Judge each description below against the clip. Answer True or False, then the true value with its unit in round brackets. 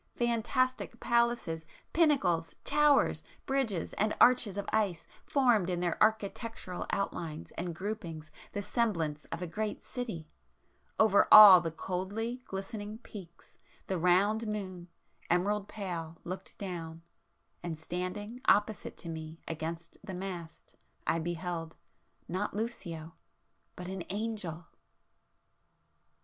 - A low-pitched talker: False (190 Hz)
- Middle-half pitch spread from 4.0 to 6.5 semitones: True (4.5 semitones)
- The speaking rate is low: True (110 wpm)